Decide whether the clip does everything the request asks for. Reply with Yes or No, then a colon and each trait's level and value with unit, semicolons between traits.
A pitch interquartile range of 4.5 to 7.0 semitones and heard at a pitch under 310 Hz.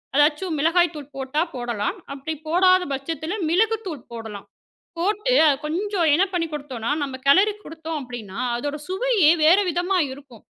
No: average, 5.0 semitones; very high, 315 Hz